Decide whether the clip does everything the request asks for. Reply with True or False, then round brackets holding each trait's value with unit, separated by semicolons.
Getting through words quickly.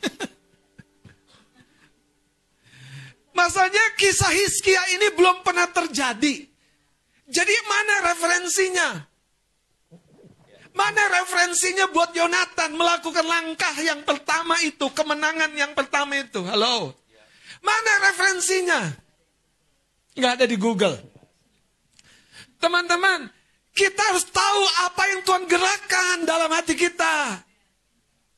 False (85 wpm)